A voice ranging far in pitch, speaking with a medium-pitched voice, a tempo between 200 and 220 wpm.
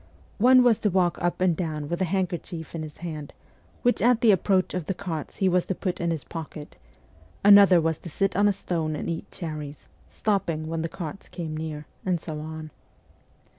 No: average, 3.4 semitones; medium, 170 Hz; fast, 205 wpm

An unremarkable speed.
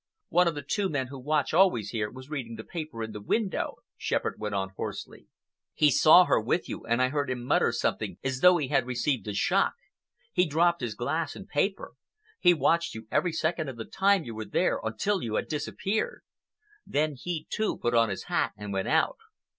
No: fast, 215 wpm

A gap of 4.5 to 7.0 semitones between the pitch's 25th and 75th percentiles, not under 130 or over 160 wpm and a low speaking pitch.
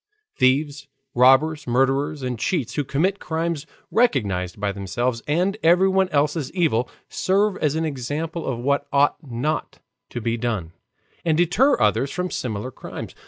No: average, 5.1 semitones; average, 150 wpm; medium, 145 Hz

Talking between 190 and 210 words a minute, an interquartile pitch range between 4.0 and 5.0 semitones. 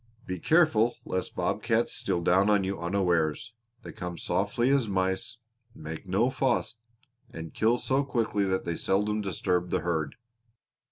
No: average, 155 wpm; average, 4.3 semitones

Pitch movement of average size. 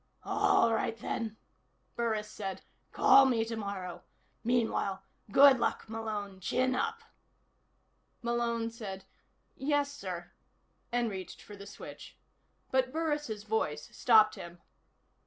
Yes: average, 4.1 semitones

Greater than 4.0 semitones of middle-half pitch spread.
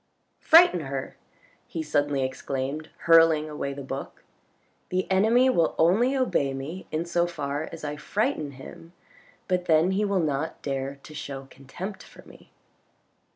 Yes: average, 4.6 semitones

